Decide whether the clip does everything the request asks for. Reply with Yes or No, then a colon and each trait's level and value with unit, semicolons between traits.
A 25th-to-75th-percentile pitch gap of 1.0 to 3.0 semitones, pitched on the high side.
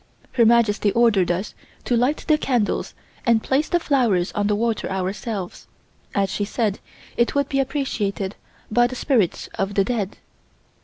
No: average, 4.0 semitones; high, 225 Hz